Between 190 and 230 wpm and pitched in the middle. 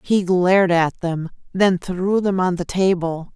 No: average, 180 wpm; medium, 180 Hz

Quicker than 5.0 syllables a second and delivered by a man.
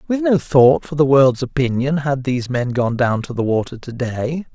No: 4.9 syllables/s; male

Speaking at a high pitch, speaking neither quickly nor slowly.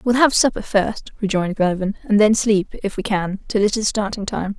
No: high, 205 Hz; fast, 220 wpm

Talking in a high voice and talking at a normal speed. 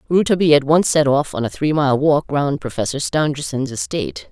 No: medium, 145 Hz; average, 195 wpm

